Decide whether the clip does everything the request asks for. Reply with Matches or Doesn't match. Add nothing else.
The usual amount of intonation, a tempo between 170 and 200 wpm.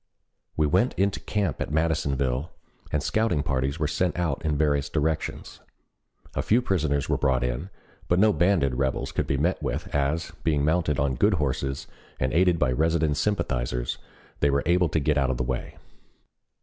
Matches